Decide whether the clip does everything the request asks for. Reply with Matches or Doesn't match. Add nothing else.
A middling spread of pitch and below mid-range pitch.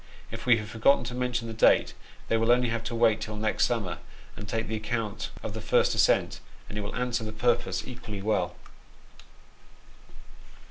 Doesn't match